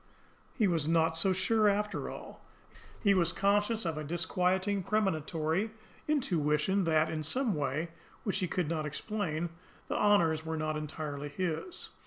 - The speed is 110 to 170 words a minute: Yes, average, 150 wpm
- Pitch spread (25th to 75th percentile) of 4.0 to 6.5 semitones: Yes, average, 4.5 semitones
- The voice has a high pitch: No, medium, 170 Hz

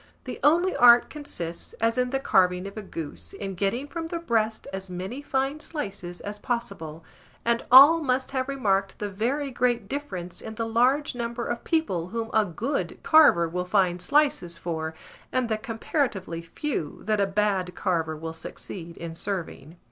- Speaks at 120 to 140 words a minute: No, average, 170 wpm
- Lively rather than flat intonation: Yes, wide, 6.3 semitones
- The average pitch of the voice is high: Yes, high, 215 Hz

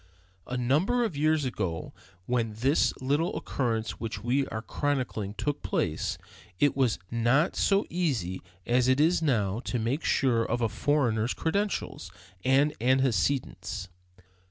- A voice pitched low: Yes, low, 130 Hz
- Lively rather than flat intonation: No, average, 4.4 semitones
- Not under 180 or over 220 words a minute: No, slow, 135 wpm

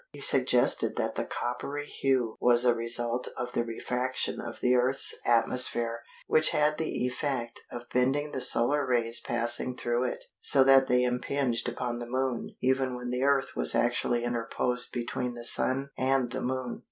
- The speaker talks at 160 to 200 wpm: Yes, average, 170 wpm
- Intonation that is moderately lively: No, narrow, 1.7 semitones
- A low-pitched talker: Yes, low, 125 Hz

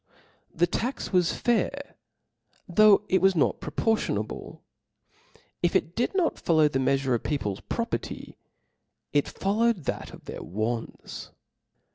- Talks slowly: Yes, slow, 130 wpm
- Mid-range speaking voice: Yes, medium, 175 Hz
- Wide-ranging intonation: Yes, wide, 8.3 semitones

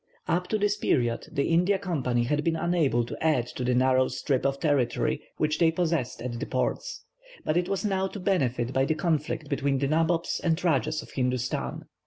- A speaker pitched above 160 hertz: No, medium, 155 Hz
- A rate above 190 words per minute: Yes, average, 200 wpm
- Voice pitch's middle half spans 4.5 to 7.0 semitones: Yes, average, 5.1 semitones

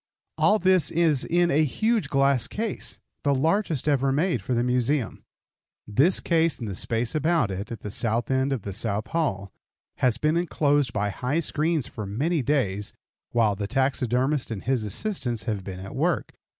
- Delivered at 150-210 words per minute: Yes, average, 175 wpm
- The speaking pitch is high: No, low, 130 Hz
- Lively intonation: Yes, wide, 6.1 semitones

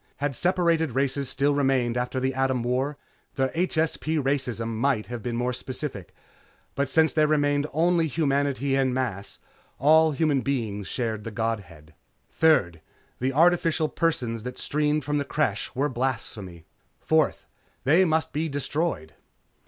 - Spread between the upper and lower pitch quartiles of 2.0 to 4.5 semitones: Yes, average, 4.1 semitones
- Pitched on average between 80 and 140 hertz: Yes, low, 135 Hz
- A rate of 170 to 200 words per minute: No, average, 145 wpm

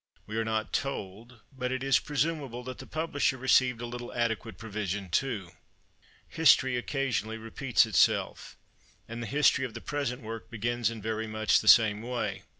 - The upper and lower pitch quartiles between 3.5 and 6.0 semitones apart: No, average, 2.9 semitones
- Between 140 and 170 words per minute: Yes, average, 165 wpm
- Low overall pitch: Yes, low, 120 Hz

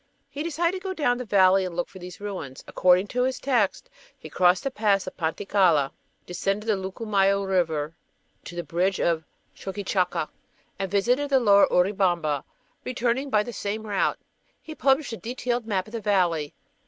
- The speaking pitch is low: No, high, 200 Hz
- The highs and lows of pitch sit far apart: No, average, 4.9 semitones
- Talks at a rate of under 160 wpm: No, average, 175 wpm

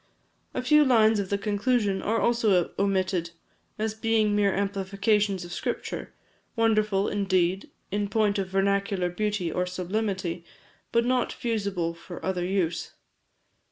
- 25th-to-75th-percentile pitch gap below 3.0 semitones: Yes, narrow, 2.5 semitones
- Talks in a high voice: Yes, high, 200 Hz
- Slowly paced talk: Yes, slow, 130 wpm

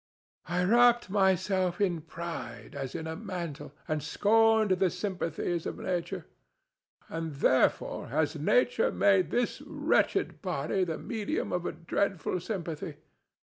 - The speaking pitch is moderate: Yes, medium, 180 Hz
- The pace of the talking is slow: Yes, slow, 130 wpm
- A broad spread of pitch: No, average, 3.9 semitones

